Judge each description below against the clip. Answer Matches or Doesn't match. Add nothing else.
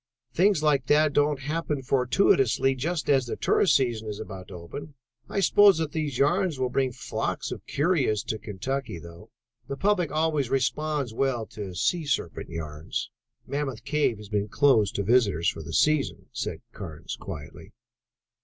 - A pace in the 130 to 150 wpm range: Doesn't match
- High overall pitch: Doesn't match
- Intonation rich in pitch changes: Matches